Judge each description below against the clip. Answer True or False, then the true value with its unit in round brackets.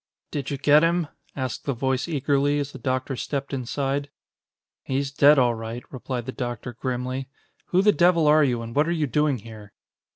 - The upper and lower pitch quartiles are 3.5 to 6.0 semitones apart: False (2.8 semitones)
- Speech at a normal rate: True (190 wpm)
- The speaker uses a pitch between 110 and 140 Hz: True (135 Hz)